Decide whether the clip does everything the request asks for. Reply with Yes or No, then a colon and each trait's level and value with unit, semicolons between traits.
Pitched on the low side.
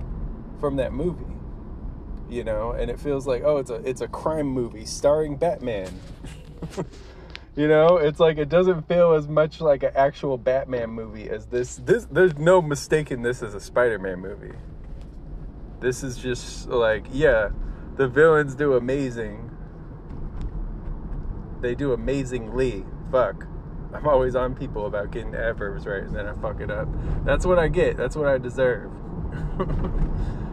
Yes: low, 130 Hz